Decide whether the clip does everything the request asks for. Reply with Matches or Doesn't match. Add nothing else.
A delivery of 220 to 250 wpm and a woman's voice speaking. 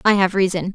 Matches